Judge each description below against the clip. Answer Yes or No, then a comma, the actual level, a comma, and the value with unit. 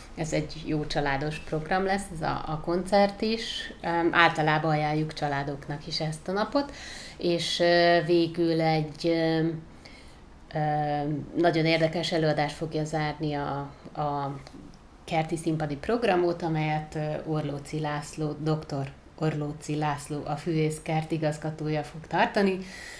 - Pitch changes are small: Yes, narrow, 2.1 semitones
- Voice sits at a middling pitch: Yes, medium, 155 Hz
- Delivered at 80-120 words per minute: Yes, average, 110 wpm